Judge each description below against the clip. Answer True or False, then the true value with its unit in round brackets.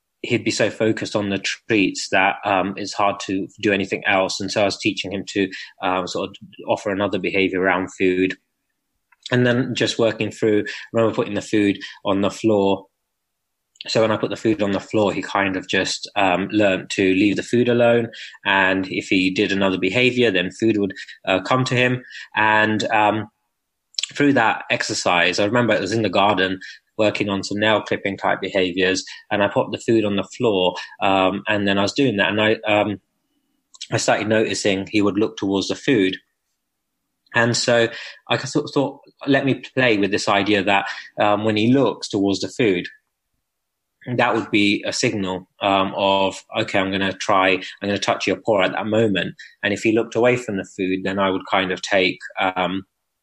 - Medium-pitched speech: False (100 Hz)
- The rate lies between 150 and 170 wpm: False (200 wpm)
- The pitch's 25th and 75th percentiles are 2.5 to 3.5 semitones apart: True (2.8 semitones)